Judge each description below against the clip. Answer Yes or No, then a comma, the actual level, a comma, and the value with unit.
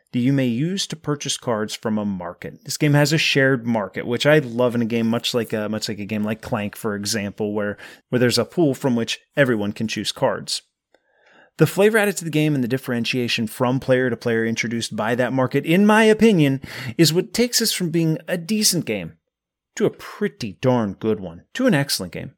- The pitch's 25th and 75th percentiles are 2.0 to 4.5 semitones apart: No, wide, 5.6 semitones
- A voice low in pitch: Yes, low, 125 Hz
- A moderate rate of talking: No, fast, 220 wpm